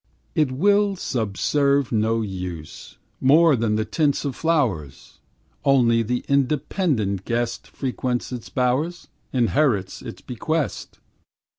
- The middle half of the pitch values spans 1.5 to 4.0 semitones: No, average, 4.9 semitones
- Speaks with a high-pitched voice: No, low, 125 Hz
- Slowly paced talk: Yes, slow, 110 wpm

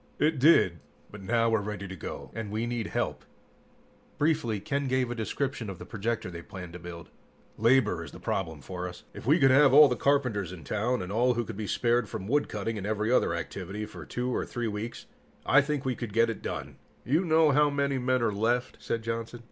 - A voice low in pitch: Yes, low, 115 Hz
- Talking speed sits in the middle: No, fast, 220 wpm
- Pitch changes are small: No, average, 4.3 semitones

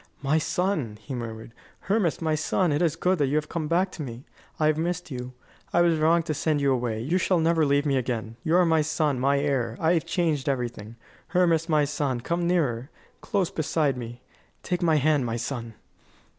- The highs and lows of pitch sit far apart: No, average, 4.6 semitones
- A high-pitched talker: No, medium, 150 Hz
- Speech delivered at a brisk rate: Yes, fast, 210 wpm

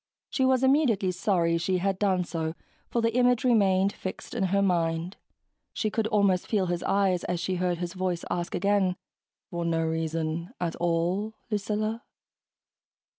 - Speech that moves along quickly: No, average, 160 wpm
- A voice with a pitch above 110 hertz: Yes, medium, 185 Hz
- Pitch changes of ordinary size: Yes, average, 3.5 semitones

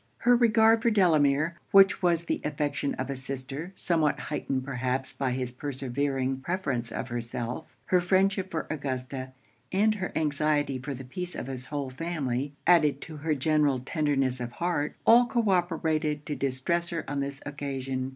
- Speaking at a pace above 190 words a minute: No, average, 165 wpm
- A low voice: No, medium, 145 Hz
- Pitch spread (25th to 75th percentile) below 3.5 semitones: No, average, 4.5 semitones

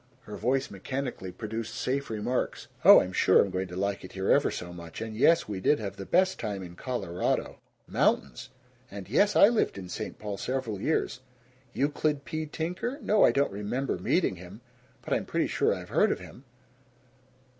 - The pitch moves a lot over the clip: Yes, wide, 6.6 semitones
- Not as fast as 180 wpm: No, average, 190 wpm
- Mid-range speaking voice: No, low, 110 Hz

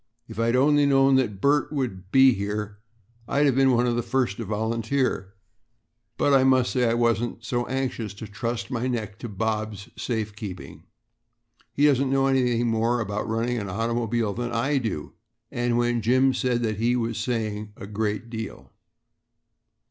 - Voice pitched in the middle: No, low, 115 Hz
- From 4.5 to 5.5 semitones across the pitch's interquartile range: No, average, 3.0 semitones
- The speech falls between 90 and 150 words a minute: No, average, 165 wpm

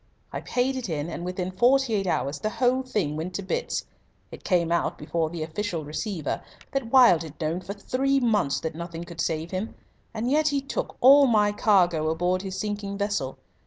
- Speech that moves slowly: No, average, 200 wpm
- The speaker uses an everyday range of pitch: No, wide, 6.2 semitones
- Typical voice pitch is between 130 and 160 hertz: No, high, 190 Hz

